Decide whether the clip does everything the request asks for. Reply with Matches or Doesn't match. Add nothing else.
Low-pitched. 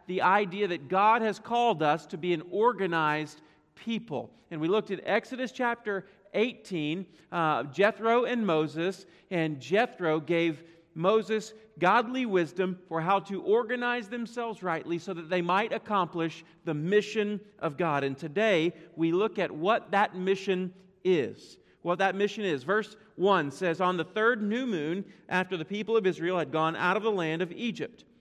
Doesn't match